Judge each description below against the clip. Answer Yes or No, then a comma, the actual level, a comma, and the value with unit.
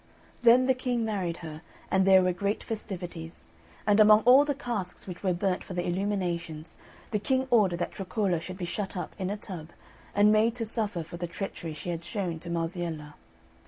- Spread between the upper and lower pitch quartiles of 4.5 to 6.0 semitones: No, average, 3.7 semitones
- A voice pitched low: No, high, 190 Hz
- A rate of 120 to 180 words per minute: No, average, 200 wpm